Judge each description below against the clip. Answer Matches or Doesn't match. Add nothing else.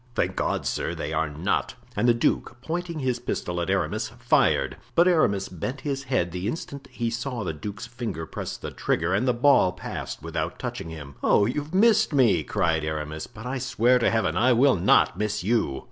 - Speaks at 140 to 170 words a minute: Doesn't match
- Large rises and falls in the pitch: Matches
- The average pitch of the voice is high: Doesn't match